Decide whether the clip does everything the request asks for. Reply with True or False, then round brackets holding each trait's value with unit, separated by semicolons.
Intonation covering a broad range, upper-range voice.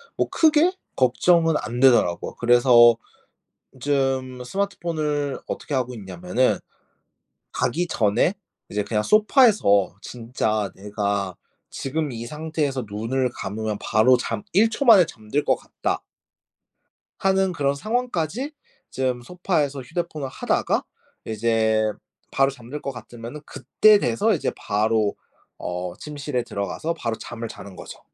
False (6.5 semitones; 130 Hz)